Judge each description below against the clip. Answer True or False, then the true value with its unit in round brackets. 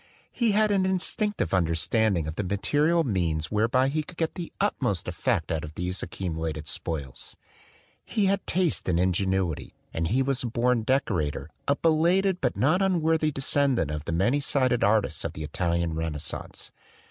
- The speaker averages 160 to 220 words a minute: True (170 wpm)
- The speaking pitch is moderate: False (115 Hz)